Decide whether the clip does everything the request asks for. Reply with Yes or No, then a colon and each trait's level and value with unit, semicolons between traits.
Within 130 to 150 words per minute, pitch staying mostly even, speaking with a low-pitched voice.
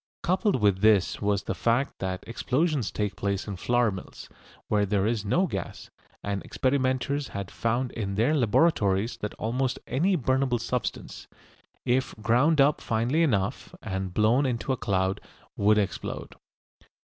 No: average, 145 wpm; average, 4.6 semitones; low, 115 Hz